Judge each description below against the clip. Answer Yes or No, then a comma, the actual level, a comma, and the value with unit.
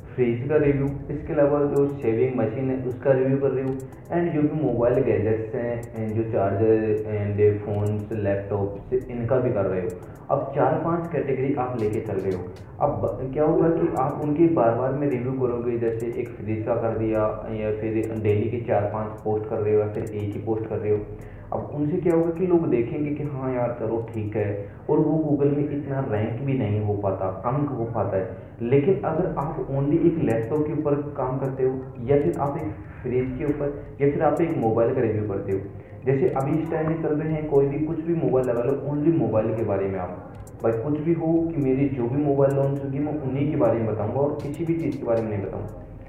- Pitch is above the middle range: No, low, 125 Hz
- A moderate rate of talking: No, fast, 230 wpm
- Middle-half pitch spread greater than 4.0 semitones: Yes, average, 5.0 semitones